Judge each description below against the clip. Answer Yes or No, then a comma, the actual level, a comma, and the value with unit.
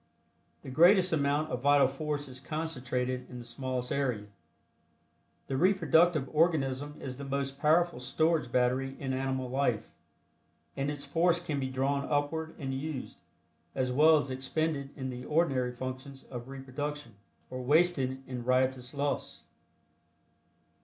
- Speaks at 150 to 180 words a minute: No, average, 140 wpm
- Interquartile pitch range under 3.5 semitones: Yes, average, 2.8 semitones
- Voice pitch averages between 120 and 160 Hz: Yes, low, 135 Hz